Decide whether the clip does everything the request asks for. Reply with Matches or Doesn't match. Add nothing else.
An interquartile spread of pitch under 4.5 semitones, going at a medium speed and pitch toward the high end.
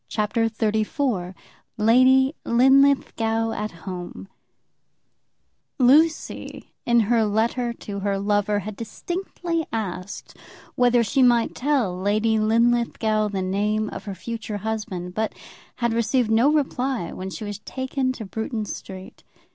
Doesn't match